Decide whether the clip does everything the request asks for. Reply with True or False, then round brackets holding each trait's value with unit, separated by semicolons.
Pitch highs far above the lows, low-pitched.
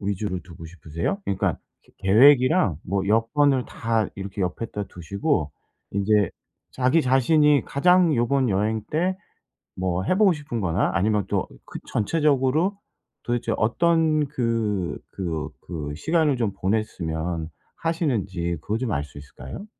True (7.7 semitones; 110 Hz)